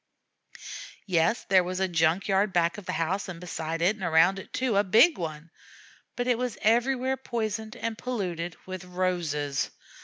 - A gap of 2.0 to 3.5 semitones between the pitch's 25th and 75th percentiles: No, average, 4.7 semitones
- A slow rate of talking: No, average, 175 wpm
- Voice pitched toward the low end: No, medium, 185 Hz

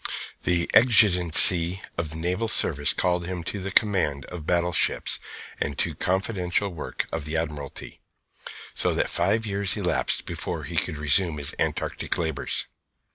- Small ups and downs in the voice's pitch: No, average, 3.5 semitones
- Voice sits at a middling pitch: No, very low, 85 Hz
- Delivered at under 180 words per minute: Yes, average, 145 wpm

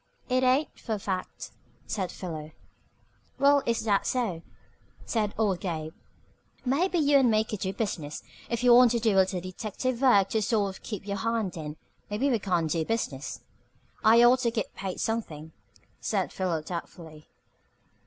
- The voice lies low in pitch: No, high, 210 Hz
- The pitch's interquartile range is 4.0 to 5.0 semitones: Yes, average, 4.7 semitones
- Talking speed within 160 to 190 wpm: Yes, average, 170 wpm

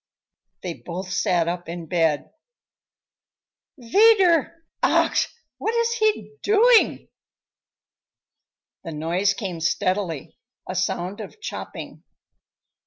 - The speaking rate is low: Yes, slow, 95 wpm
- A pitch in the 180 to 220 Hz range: Yes, high, 190 Hz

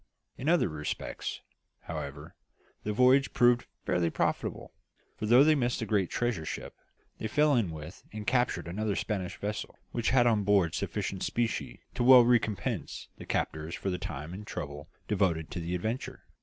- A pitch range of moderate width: No, wide, 6.0 semitones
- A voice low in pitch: Yes, low, 105 Hz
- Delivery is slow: No, average, 170 wpm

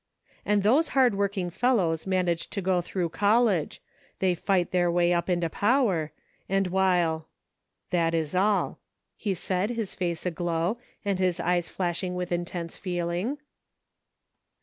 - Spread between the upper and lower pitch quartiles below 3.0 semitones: Yes, narrow, 2.5 semitones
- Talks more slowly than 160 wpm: Yes, average, 150 wpm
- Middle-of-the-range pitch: Yes, medium, 180 Hz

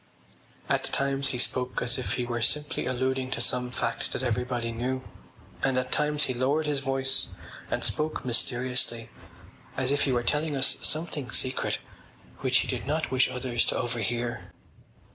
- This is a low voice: Yes, low, 130 Hz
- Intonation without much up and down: Yes, narrow, 2.1 semitones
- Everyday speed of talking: Yes, average, 165 wpm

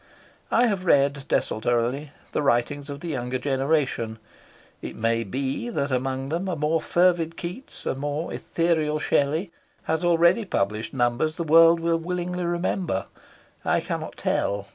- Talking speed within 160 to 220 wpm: No, average, 145 wpm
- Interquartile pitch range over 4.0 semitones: Yes, average, 4.5 semitones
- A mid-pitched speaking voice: Yes, medium, 150 Hz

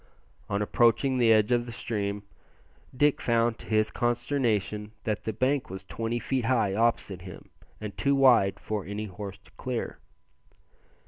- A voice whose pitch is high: No, low, 115 Hz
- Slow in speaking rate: No, average, 155 wpm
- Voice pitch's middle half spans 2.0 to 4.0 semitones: Yes, average, 2.9 semitones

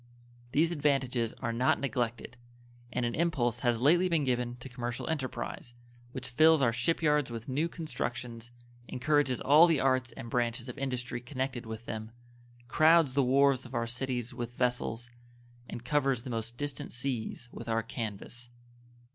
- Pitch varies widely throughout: No, average, 2.7 semitones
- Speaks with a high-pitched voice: No, low, 125 Hz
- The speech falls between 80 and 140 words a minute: No, average, 160 wpm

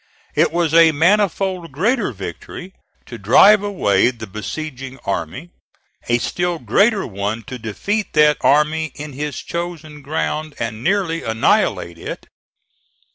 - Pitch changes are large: Yes, wide, 7.1 semitones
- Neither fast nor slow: No, slow, 130 wpm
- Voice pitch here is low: No, medium, 150 Hz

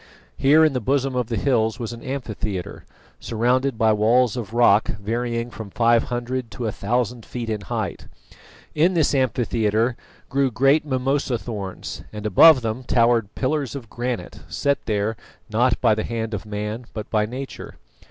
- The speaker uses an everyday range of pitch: Yes, average, 3.0 semitones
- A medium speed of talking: Yes, average, 165 wpm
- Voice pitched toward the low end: Yes, low, 120 Hz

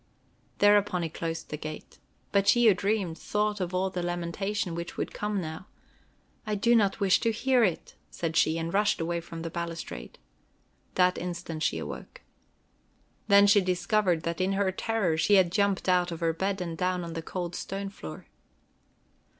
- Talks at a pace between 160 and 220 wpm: Yes, average, 180 wpm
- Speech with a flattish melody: No, average, 3.2 semitones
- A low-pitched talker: No, medium, 185 Hz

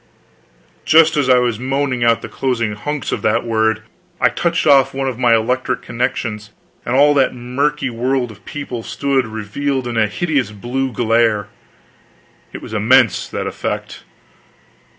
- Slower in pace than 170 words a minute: Yes, average, 155 wpm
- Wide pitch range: No, average, 3.2 semitones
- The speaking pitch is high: No, low, 125 Hz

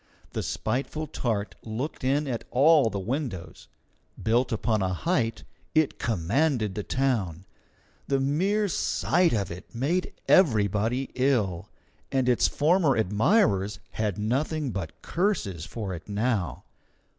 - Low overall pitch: Yes, low, 120 Hz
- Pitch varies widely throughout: Yes, wide, 5.9 semitones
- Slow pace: Yes, slow, 125 wpm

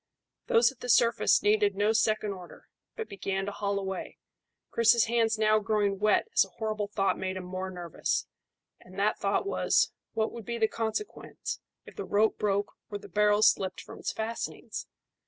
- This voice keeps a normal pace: Yes, average, 180 wpm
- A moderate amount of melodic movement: No, narrow, 2.1 semitones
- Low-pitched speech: No, high, 210 Hz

